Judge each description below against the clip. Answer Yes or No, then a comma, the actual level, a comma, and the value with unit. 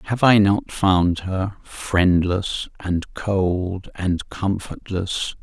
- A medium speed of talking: No, slow, 110 wpm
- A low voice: Yes, very low, 95 Hz